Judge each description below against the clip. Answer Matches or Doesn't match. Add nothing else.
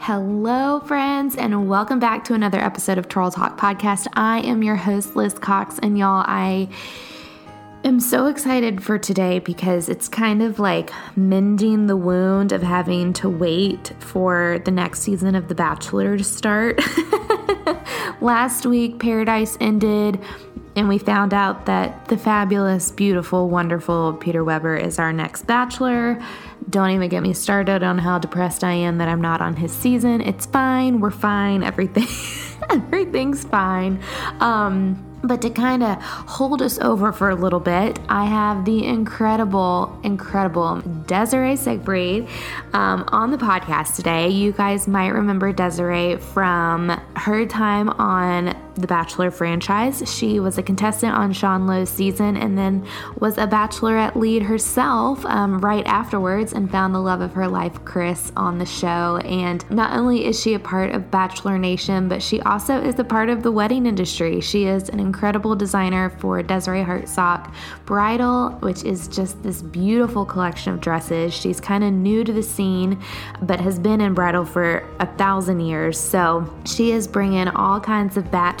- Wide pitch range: Doesn't match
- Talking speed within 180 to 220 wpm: Doesn't match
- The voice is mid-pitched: Doesn't match